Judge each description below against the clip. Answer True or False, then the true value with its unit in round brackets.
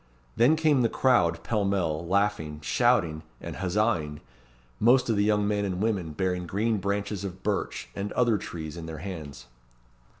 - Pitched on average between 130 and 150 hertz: False (100 Hz)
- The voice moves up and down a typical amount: True (4.2 semitones)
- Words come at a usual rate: True (160 wpm)